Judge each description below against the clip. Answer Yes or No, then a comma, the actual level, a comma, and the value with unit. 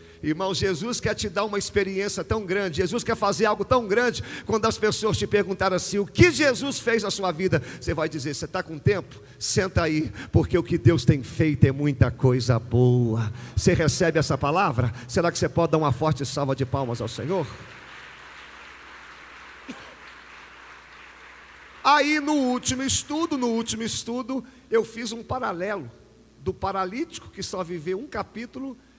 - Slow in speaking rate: No, average, 170 wpm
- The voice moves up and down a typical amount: No, wide, 7.6 semitones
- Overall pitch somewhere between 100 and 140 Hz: No, medium, 185 Hz